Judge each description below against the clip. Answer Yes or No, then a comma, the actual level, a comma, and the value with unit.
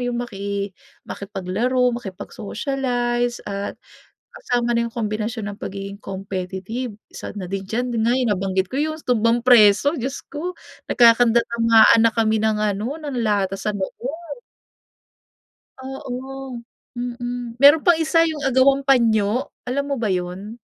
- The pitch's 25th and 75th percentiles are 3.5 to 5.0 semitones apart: Yes, average, 4.1 semitones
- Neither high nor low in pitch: No, high, 235 Hz